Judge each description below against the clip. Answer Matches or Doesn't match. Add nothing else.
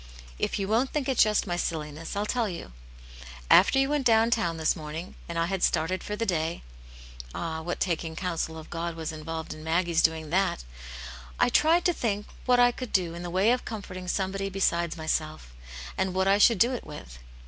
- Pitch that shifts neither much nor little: Matches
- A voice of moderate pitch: Matches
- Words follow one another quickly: Matches